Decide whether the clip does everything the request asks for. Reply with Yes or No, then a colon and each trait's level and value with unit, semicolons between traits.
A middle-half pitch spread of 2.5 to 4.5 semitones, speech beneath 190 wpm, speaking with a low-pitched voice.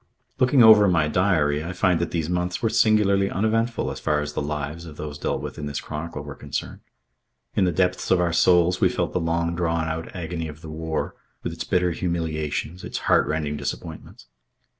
No: average, 2.8 semitones; average, 200 wpm; very low, 85 Hz